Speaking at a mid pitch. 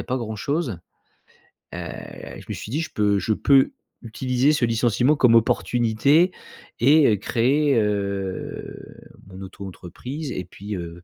No: low, 115 Hz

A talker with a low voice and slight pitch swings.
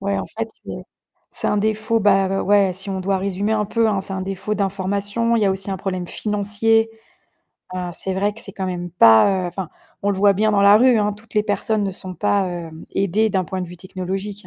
No: high, 195 Hz; narrow, 1.8 semitones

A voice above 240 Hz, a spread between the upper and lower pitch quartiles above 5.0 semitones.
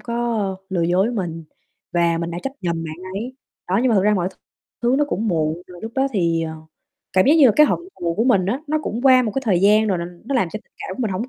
No: high, 195 Hz; wide, 5.5 semitones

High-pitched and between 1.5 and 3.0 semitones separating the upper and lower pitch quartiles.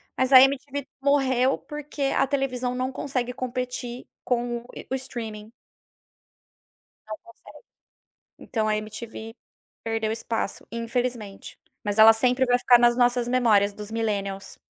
Yes: high, 245 Hz; narrow, 2.6 semitones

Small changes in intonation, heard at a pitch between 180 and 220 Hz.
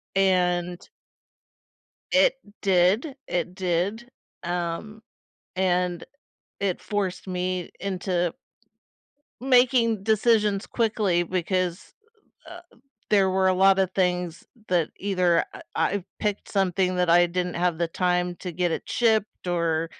Yes: narrow, 2.3 semitones; medium, 185 Hz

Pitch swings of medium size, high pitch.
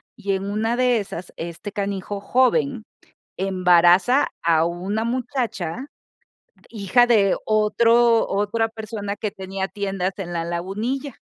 Yes: average, 3.6 semitones; high, 205 Hz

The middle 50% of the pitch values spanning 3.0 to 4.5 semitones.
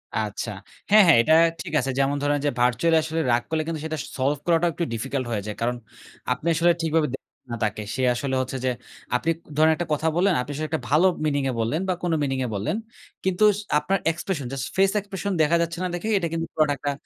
Yes: average, 4.1 semitones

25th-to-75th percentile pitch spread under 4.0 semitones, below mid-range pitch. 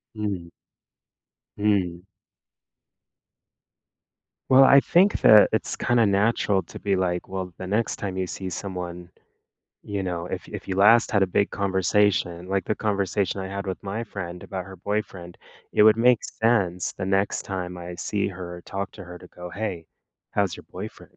Yes: narrow, 2.5 semitones; very low, 95 Hz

